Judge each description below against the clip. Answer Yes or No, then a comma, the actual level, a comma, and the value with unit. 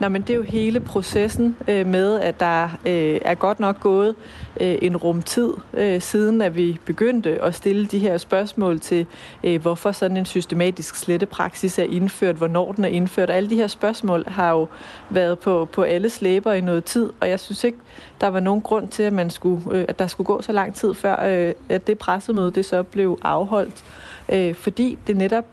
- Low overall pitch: No, high, 190 Hz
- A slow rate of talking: No, average, 210 wpm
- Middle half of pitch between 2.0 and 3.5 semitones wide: Yes, average, 2.8 semitones